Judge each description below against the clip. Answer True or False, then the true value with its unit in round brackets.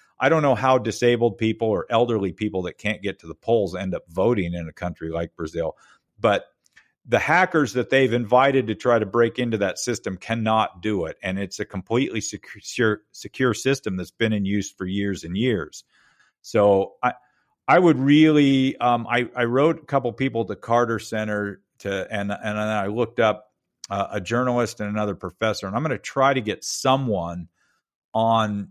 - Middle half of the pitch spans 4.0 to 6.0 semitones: False (3.6 semitones)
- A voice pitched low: True (110 Hz)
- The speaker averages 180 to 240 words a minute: True (190 wpm)